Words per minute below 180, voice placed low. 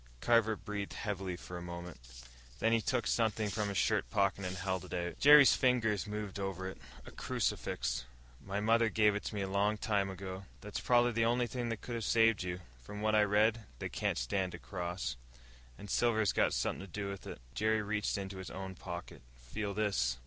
No: fast, 205 wpm; low, 100 Hz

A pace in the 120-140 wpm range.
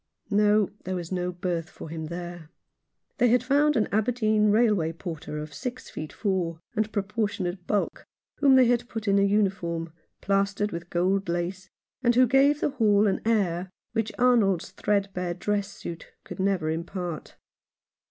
No: average, 160 wpm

